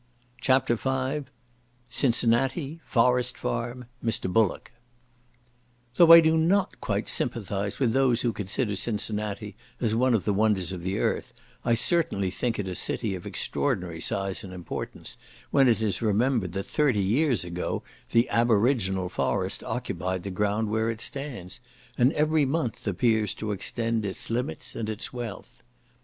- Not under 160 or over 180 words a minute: No, average, 145 wpm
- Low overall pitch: Yes, low, 115 Hz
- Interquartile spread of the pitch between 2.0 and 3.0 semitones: No, average, 4.3 semitones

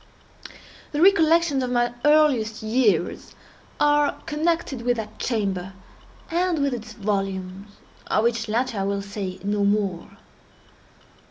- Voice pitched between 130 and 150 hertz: No, high, 225 Hz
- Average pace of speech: No, slow, 115 wpm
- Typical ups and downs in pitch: No, wide, 6.5 semitones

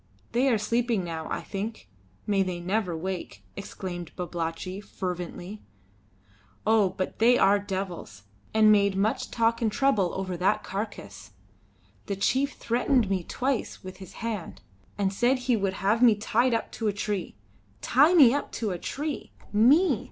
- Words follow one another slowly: No, average, 160 wpm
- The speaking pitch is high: Yes, high, 205 Hz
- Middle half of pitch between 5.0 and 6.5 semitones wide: No, average, 3.9 semitones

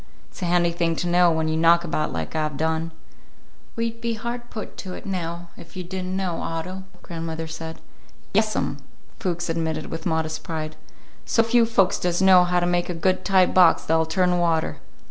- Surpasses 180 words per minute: Yes, average, 200 wpm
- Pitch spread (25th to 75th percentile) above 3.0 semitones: No, narrow, 2.4 semitones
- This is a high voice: No, medium, 175 Hz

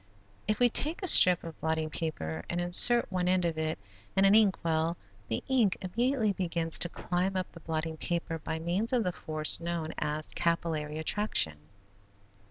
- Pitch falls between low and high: Yes, medium, 170 Hz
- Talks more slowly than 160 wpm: No, average, 180 wpm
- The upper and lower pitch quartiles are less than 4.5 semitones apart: Yes, average, 3.4 semitones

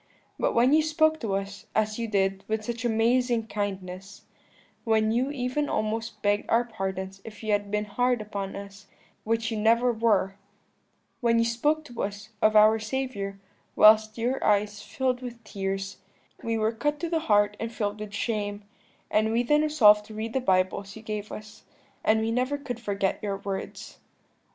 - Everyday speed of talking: Yes, average, 180 wpm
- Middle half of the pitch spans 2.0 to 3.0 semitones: Yes, average, 2.7 semitones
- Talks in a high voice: Yes, high, 220 Hz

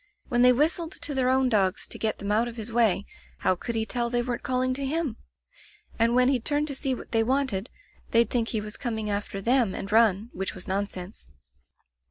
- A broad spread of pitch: No, average, 3.5 semitones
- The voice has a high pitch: Yes, high, 235 Hz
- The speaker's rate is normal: No, fast, 220 wpm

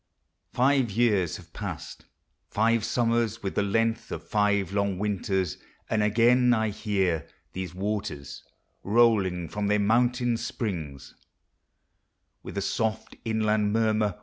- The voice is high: No, low, 105 Hz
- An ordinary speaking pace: No, slow, 120 wpm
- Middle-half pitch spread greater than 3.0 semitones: No, average, 2.7 semitones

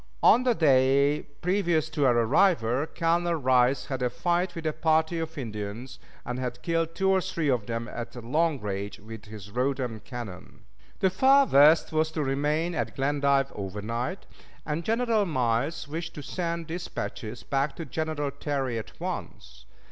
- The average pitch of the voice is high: No, medium, 145 Hz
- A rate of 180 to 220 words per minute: No, average, 165 wpm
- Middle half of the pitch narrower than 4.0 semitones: No, average, 5.3 semitones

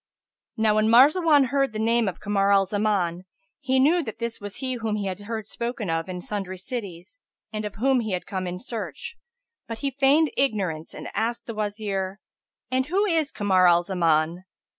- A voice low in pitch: No, high, 215 Hz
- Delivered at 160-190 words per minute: Yes, average, 185 wpm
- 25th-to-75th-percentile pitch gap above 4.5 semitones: Yes, average, 5.2 semitones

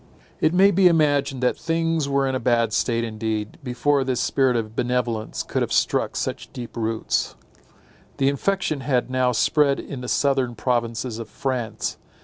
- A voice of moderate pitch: No, low, 130 Hz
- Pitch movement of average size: Yes, average, 3.2 semitones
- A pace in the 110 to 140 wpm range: No, average, 165 wpm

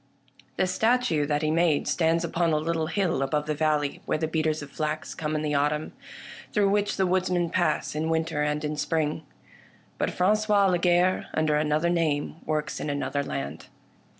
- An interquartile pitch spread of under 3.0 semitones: Yes, narrow, 2.6 semitones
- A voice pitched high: No, medium, 155 Hz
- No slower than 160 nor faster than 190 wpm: Yes, average, 180 wpm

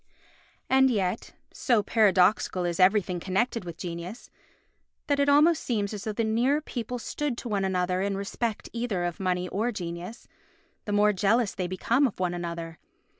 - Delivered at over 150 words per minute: Yes, average, 170 wpm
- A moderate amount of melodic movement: Yes, average, 4.5 semitones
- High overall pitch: Yes, high, 205 Hz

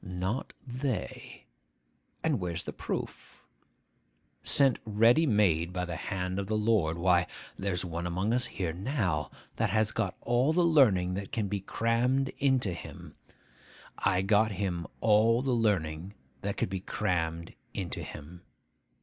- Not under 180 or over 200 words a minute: No, average, 145 wpm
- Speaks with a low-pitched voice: Yes, low, 100 Hz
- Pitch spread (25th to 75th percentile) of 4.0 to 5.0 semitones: Yes, average, 4.5 semitones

